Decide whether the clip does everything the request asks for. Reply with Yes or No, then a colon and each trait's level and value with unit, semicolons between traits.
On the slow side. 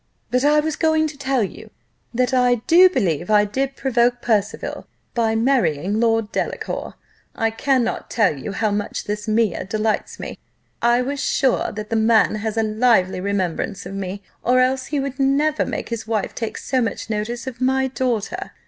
No: average, 180 wpm